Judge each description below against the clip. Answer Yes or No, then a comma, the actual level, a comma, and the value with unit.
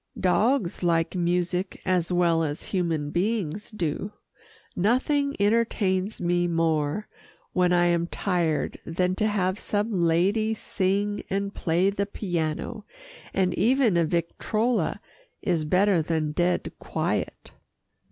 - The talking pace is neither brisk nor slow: No, slow, 120 wpm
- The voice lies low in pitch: No, medium, 180 Hz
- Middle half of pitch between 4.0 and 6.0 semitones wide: No, average, 3.3 semitones